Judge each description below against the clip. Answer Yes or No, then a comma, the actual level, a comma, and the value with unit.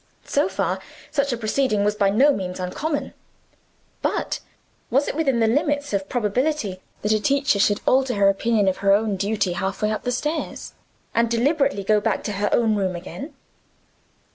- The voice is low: No, high, 220 Hz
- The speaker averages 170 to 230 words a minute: Yes, average, 180 wpm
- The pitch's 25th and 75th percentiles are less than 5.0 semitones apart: No, average, 5.3 semitones